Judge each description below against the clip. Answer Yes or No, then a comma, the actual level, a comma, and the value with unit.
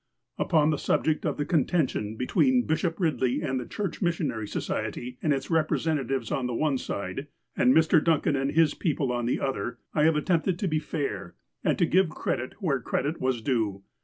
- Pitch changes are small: No, average, 4.3 semitones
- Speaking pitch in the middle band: Yes, medium, 145 Hz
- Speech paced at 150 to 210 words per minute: Yes, average, 190 wpm